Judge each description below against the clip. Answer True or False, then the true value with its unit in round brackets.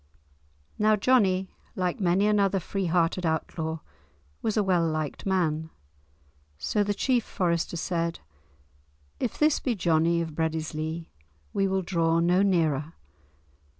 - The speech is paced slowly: True (125 wpm)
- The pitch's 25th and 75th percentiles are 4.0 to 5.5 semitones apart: False (3.3 semitones)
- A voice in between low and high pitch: True (175 Hz)